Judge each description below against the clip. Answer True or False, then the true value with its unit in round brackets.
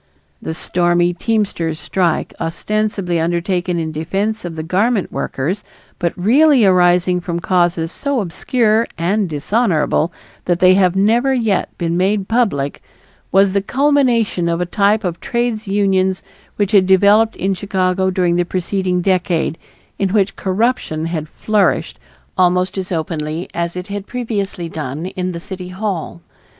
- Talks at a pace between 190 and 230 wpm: False (145 wpm)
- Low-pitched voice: False (185 Hz)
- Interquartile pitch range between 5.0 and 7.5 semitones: False (3.2 semitones)